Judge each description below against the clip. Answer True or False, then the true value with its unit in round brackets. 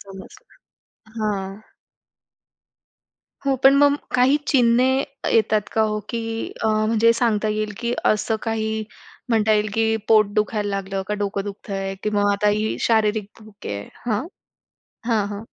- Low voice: False (215 Hz)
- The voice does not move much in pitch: True (1.6 semitones)